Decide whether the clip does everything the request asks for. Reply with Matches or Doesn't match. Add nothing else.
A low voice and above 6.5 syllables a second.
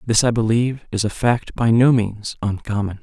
Doesn't match